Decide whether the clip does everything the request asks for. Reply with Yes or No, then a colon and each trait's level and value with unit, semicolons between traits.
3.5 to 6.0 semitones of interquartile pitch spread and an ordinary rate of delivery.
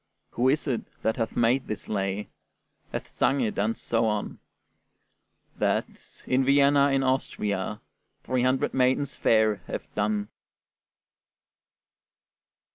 No: average, 3.9 semitones; slow, 115 wpm